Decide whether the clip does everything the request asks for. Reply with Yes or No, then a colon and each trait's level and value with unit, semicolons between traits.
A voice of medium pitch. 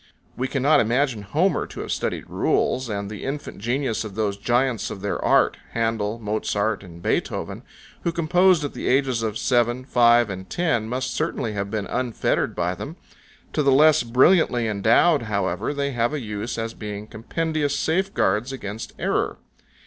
No: low, 120 Hz